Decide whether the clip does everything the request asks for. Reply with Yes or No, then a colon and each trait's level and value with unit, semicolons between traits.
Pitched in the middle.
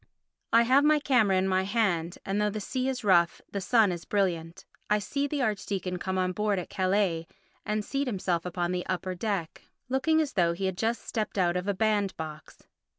No: high, 195 Hz